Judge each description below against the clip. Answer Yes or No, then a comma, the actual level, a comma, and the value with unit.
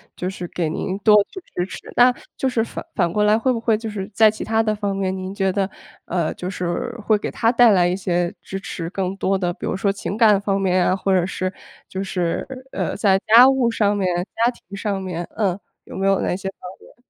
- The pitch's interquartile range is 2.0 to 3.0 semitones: Yes, narrow, 2.6 semitones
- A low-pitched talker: No, high, 195 Hz